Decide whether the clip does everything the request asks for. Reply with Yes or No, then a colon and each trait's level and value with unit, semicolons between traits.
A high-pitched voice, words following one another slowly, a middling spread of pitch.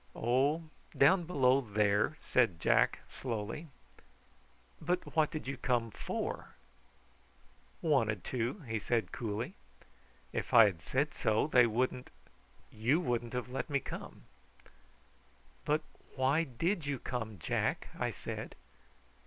No: low, 125 Hz; slow, 120 wpm; average, 4.7 semitones